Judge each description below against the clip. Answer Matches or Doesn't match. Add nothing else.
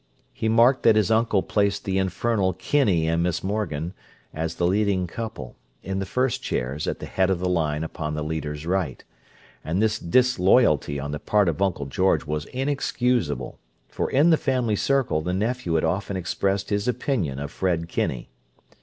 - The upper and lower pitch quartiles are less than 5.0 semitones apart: Doesn't match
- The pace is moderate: Matches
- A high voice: Doesn't match